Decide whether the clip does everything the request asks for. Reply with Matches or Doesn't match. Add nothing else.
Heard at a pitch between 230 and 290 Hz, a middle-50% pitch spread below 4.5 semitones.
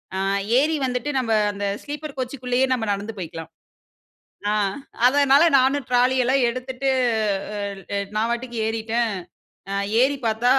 Matches